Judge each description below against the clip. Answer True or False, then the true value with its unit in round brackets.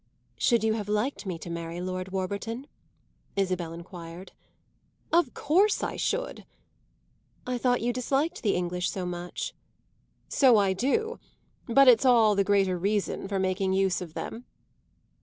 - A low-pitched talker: False (200 Hz)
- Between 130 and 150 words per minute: True (145 wpm)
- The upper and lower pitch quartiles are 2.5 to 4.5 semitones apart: False (5.1 semitones)